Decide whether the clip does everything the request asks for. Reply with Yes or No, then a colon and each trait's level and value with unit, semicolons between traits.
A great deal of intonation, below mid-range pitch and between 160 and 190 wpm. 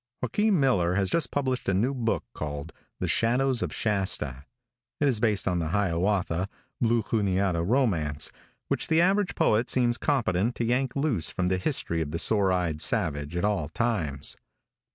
Yes: wide, 6.5 semitones; low, 100 Hz; average, 170 wpm